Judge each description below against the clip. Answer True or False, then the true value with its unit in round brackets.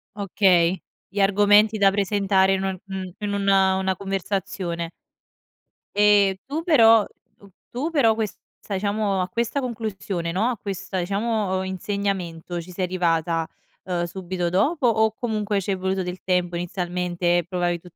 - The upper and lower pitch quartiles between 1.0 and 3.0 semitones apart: True (2.5 semitones)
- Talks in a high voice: True (195 Hz)